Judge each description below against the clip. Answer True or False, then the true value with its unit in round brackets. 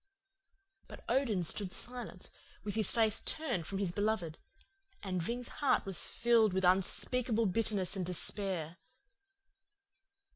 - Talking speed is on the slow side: True (120 wpm)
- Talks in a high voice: True (205 Hz)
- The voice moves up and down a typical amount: True (4.0 semitones)